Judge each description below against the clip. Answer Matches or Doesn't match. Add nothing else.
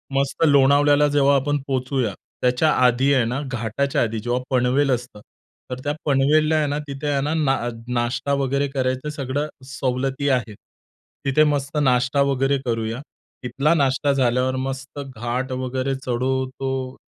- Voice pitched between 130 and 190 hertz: Matches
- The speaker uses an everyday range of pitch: Doesn't match